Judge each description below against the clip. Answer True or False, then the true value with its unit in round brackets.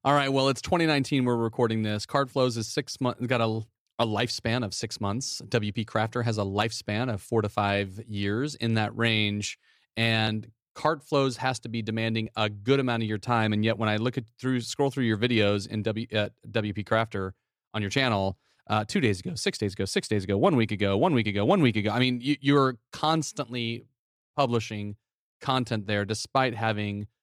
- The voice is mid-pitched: False (115 Hz)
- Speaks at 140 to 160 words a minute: False (205 wpm)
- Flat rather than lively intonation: False (3.0 semitones)